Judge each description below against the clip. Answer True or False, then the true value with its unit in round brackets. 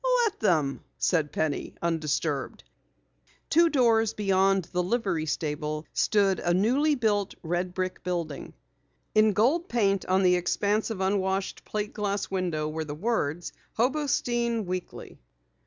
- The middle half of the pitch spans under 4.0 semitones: False (4.5 semitones)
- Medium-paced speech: False (130 wpm)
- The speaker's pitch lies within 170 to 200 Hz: True (190 Hz)